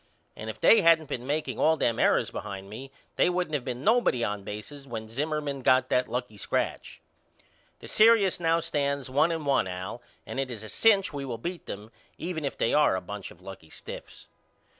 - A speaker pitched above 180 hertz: No, low, 135 Hz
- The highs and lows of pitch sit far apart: Yes, wide, 6.4 semitones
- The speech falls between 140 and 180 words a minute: No, fast, 205 wpm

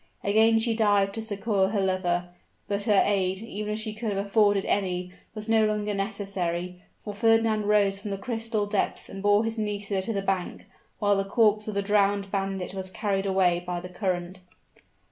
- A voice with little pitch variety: Yes, narrow, 1.8 semitones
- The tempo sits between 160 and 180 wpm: No, average, 190 wpm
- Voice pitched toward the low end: No, high, 200 Hz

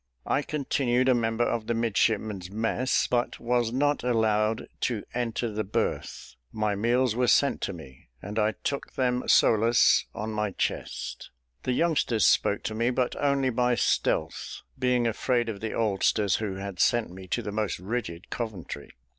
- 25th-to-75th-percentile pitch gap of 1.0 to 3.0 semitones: Yes, average, 2.7 semitones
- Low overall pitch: Yes, low, 115 Hz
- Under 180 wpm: Yes, average, 165 wpm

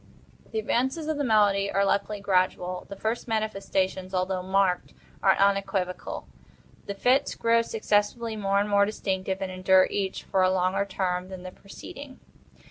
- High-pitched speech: Yes, high, 195 Hz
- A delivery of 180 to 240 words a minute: No, average, 155 wpm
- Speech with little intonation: Yes, narrow, 2.3 semitones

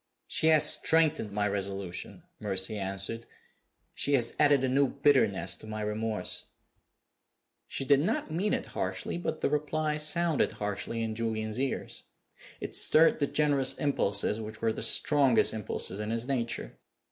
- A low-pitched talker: Yes, low, 115 Hz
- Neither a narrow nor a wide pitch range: No, wide, 5.8 semitones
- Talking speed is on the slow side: No, average, 150 wpm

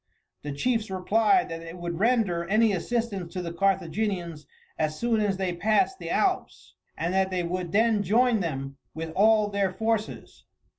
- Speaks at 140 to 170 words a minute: Yes, average, 165 wpm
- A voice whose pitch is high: Yes, high, 195 Hz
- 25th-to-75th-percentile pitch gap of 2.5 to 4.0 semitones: No, average, 4.5 semitones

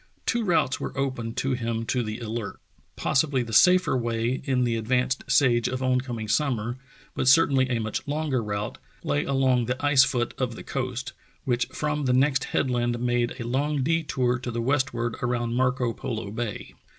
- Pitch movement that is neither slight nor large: No, narrow, 2.3 semitones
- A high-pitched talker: No, low, 125 Hz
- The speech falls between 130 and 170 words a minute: No, average, 180 wpm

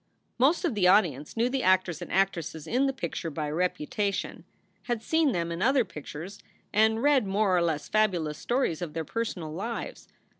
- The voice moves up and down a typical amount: No, wide, 5.7 semitones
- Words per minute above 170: Yes, average, 180 wpm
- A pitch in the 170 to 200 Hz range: Yes, high, 190 Hz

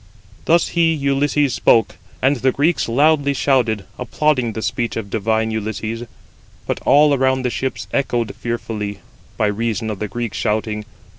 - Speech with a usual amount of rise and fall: Yes, average, 4.1 semitones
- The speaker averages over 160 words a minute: No, average, 150 wpm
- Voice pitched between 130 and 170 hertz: No, low, 120 Hz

